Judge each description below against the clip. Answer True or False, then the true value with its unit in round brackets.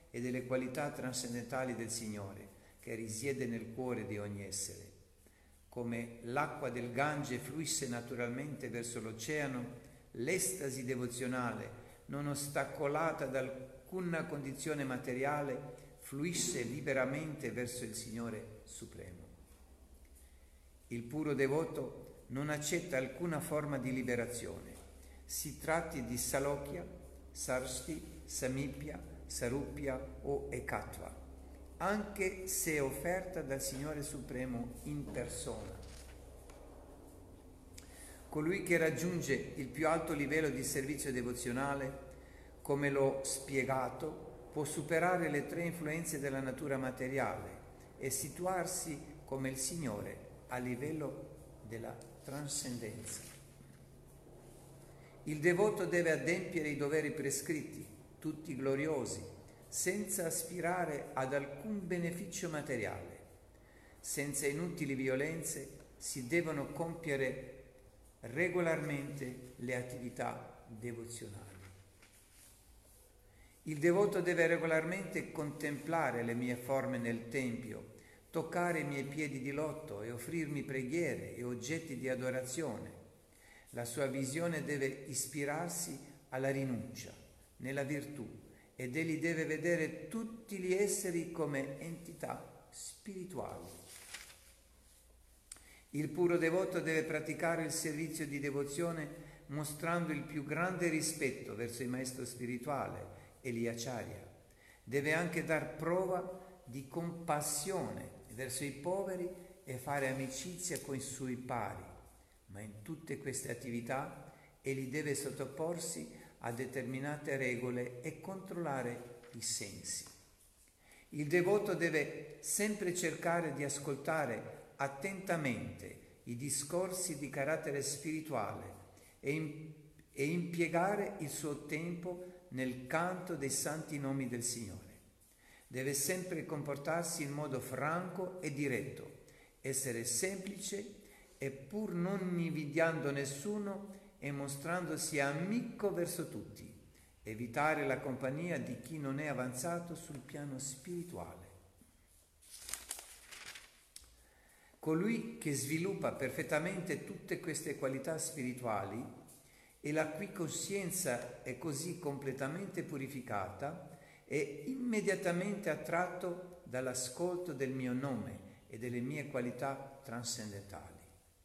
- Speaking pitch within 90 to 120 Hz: False (140 Hz)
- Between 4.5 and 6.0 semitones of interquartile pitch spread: True (4.9 semitones)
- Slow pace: True (100 wpm)